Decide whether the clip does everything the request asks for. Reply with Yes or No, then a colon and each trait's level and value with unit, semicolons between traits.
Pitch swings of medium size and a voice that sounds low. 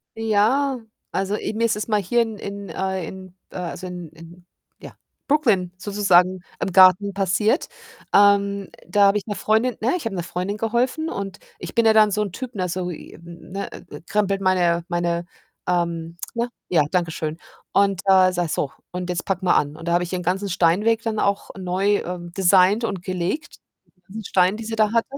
No: average, 3.0 semitones; high, 195 Hz